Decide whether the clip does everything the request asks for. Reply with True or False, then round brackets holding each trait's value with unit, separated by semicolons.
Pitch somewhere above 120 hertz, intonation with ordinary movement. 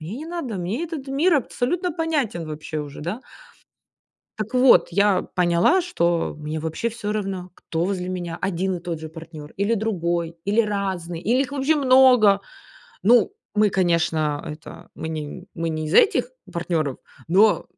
False (190 Hz; 6.6 semitones)